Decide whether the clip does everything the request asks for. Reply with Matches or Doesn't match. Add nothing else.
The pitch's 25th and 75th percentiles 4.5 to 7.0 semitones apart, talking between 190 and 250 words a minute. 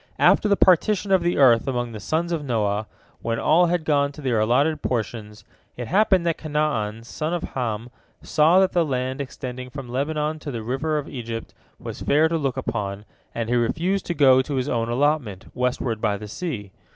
Matches